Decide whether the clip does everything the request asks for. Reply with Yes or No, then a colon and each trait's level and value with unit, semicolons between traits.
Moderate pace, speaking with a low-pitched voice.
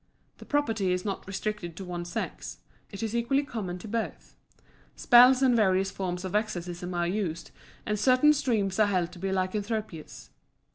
No: average, 165 wpm; high, 200 Hz